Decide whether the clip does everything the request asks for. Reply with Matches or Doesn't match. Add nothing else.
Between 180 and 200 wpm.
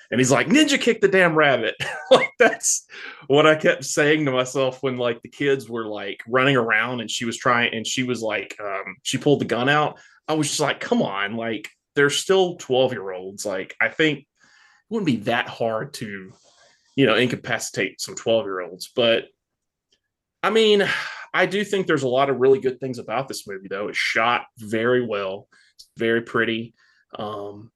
Matches